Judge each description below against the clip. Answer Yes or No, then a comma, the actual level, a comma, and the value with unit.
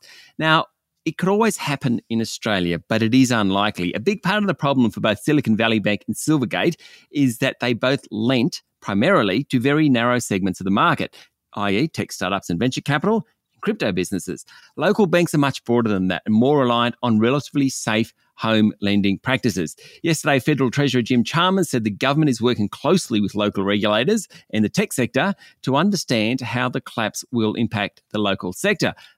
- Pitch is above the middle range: No, low, 125 Hz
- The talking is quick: No, average, 185 wpm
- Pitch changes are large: Yes, wide, 5.9 semitones